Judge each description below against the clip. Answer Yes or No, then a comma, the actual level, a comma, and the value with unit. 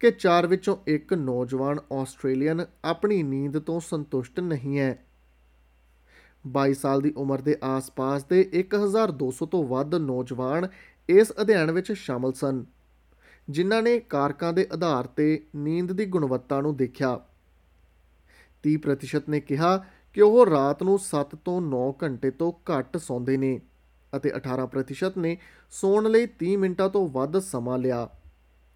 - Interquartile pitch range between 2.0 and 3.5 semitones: No, wide, 5.6 semitones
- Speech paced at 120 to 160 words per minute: Yes, average, 135 wpm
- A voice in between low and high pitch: Yes, medium, 145 Hz